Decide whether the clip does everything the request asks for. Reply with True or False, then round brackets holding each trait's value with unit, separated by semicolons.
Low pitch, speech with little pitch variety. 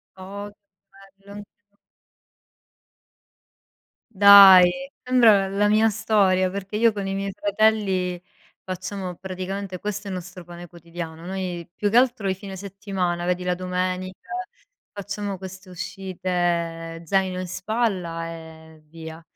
False (190 Hz; 2.2 semitones)